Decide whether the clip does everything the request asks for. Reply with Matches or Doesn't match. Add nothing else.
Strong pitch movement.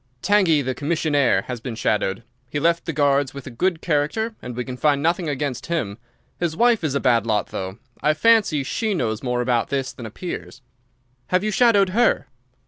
Matches